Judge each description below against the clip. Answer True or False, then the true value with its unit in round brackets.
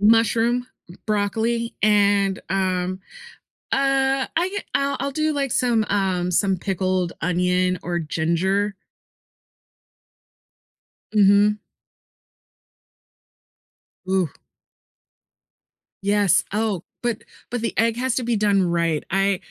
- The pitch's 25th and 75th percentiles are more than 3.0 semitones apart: True (4.0 semitones)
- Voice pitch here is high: True (205 Hz)